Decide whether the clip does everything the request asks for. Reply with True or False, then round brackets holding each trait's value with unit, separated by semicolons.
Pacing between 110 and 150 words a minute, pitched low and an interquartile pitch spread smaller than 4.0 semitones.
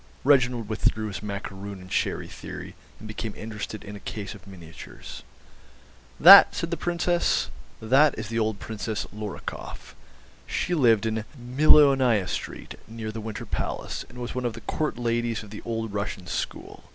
False (165 wpm; 110 Hz; 2.9 semitones)